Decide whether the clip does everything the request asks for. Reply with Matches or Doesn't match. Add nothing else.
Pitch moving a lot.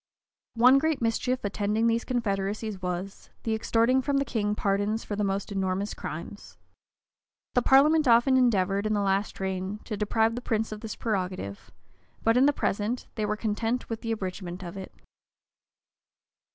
Doesn't match